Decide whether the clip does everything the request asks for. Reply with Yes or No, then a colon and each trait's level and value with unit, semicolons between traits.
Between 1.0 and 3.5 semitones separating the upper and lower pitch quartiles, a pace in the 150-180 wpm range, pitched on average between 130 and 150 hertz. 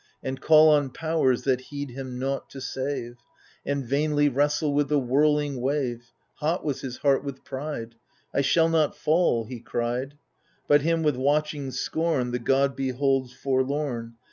Yes: narrow, 2.4 semitones; average, 160 wpm; medium, 140 Hz